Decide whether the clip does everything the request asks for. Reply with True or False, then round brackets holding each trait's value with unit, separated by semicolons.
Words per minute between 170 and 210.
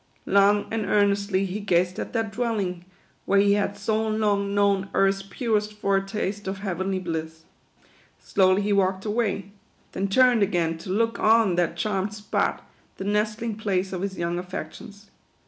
False (160 wpm)